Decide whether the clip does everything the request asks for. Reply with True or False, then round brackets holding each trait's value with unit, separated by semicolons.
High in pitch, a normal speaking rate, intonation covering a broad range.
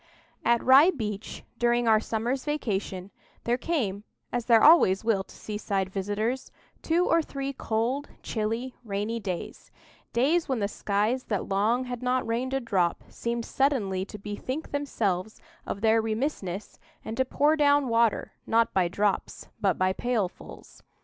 False (230 Hz; 150 wpm; 4.2 semitones)